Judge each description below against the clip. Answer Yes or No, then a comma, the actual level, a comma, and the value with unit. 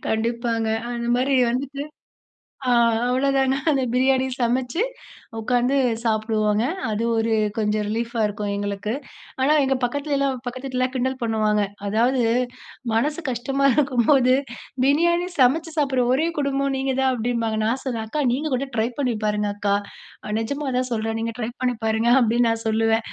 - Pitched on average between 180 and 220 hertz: No, high, 245 Hz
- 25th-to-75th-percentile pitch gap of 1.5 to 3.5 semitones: Yes, average, 3.2 semitones